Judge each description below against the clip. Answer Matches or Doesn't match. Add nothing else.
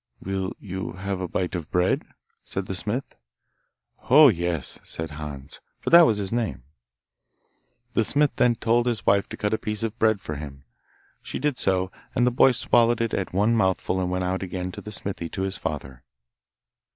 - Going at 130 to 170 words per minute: Doesn't match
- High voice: Doesn't match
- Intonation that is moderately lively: Matches